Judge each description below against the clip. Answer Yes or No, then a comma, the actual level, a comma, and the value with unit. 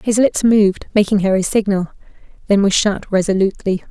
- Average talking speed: Yes, average, 170 wpm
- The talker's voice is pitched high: Yes, high, 200 Hz